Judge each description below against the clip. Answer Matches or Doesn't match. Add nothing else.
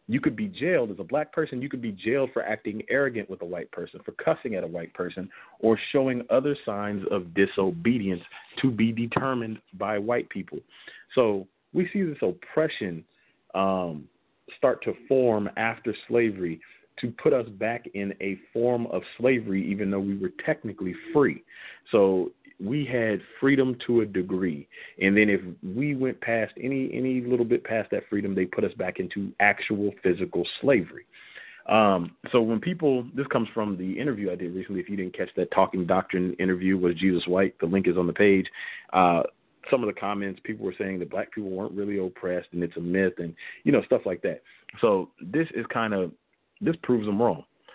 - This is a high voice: Doesn't match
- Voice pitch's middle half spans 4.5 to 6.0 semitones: Matches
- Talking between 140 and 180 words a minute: Doesn't match